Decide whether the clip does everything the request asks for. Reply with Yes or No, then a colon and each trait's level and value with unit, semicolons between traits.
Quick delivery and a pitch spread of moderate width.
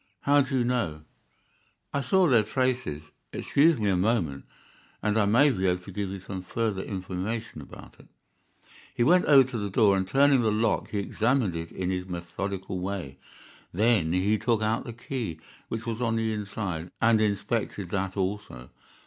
No: average, 180 wpm; average, 4.2 semitones